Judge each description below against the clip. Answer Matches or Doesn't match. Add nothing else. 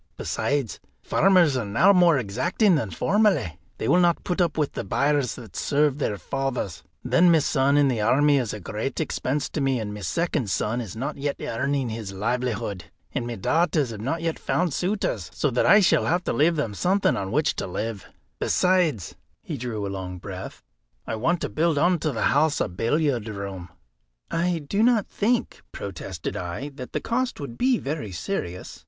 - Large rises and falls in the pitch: Matches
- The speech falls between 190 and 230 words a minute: Matches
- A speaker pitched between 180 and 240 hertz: Doesn't match